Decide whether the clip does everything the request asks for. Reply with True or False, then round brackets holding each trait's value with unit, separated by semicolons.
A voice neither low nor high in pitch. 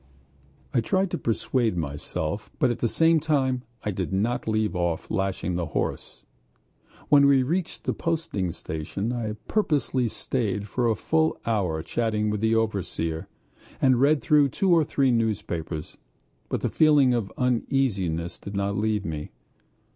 False (110 Hz)